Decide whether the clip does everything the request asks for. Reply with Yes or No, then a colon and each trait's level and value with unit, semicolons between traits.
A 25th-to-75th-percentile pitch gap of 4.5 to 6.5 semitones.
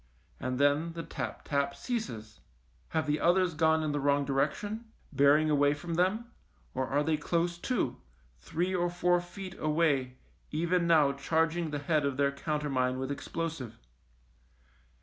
No: average, 3.4 semitones